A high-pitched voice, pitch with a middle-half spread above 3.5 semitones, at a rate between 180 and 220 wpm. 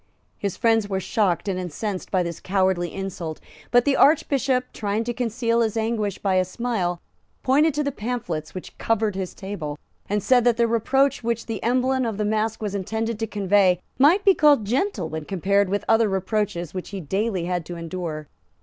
Yes: high, 210 Hz; average, 4.1 semitones; average, 190 wpm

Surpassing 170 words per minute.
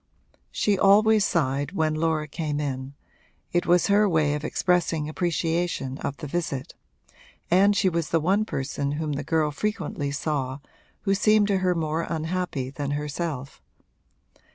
No: average, 150 wpm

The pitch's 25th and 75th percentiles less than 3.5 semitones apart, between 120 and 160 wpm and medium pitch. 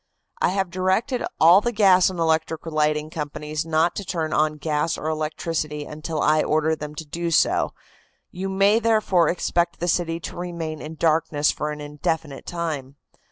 No: narrow, 2.5 semitones; average, 170 wpm; medium, 160 Hz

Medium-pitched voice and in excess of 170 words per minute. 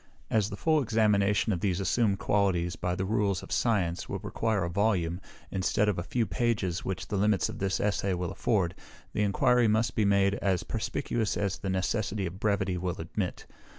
No: low, 100 Hz; average, 190 wpm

